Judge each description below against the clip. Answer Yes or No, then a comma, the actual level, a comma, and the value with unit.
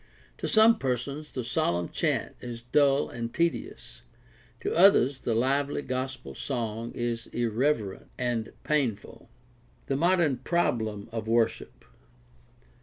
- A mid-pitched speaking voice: No, low, 125 Hz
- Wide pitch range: No, average, 3.8 semitones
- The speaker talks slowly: Yes, slow, 115 wpm